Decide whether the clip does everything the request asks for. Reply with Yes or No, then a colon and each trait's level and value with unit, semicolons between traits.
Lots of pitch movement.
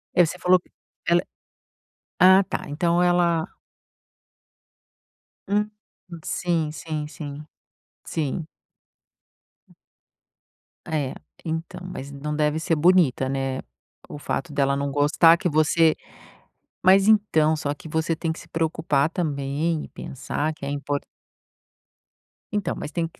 No: average, 3.0 semitones